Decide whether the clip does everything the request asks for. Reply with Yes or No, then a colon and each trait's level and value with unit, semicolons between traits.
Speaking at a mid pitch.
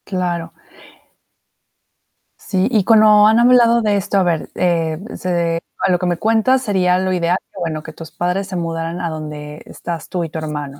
Yes: medium, 180 Hz